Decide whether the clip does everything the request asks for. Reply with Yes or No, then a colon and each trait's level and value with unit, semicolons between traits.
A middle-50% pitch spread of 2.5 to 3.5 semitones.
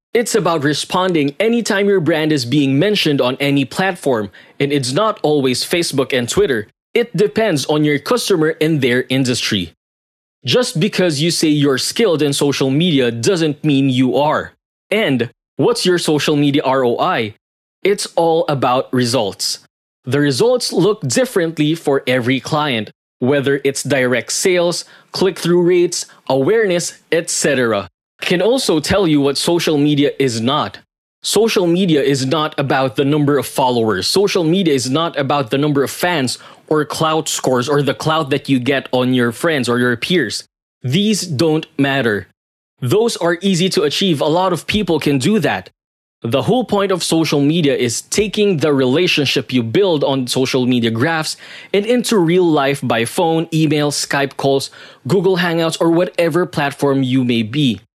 No: average, 4.5 semitones